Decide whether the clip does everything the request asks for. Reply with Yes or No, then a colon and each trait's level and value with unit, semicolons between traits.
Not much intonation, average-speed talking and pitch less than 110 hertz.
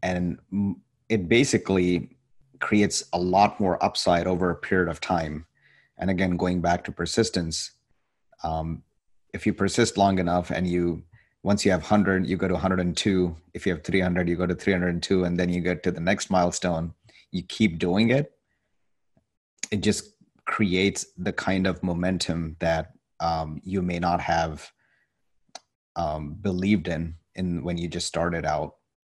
Yes: narrow, 1.9 semitones; average, 170 wpm; very low, 90 Hz